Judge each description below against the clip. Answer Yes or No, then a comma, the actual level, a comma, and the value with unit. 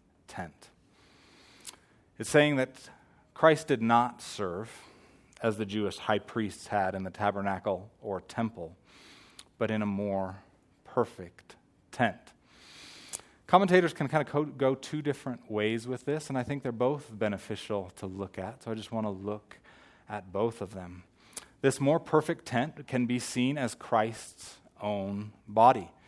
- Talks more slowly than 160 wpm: Yes, average, 150 wpm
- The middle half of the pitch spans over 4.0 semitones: Yes, average, 4.9 semitones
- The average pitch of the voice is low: Yes, low, 115 Hz